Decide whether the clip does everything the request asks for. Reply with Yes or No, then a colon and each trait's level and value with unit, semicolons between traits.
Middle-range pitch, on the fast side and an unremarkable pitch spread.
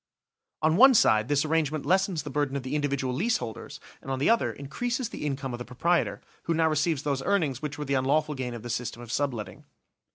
Yes: medium, 145 Hz; fast, 225 wpm; average, 3.7 semitones